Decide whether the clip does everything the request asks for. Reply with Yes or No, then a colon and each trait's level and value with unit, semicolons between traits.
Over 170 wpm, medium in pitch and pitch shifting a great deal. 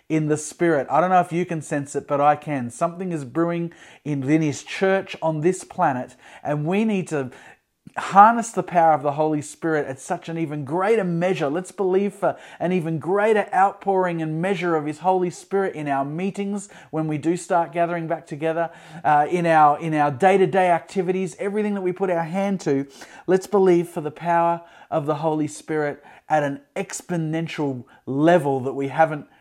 No: average, 190 wpm; medium, 170 Hz; average, 3.5 semitones